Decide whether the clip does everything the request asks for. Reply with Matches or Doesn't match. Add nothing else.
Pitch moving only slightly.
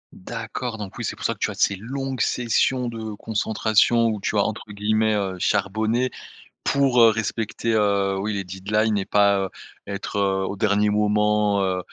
Matches